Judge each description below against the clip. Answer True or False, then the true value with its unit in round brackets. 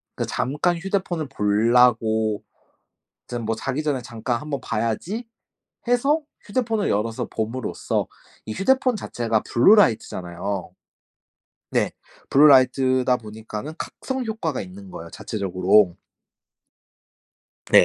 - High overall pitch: False (125 Hz)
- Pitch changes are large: True (8.2 semitones)